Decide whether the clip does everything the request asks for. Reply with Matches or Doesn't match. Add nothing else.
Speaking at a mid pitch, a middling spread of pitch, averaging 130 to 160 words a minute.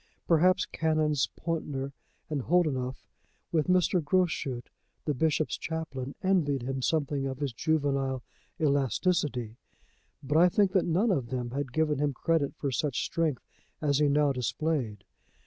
Matches